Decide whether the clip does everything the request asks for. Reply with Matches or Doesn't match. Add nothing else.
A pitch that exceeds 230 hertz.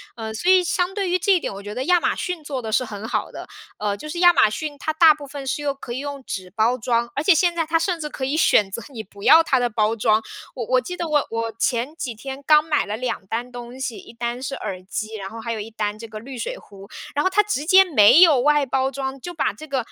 Matches